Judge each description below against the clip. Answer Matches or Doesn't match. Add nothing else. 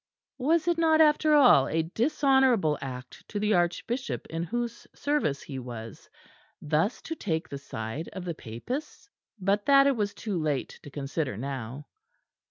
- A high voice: Doesn't match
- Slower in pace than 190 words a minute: Matches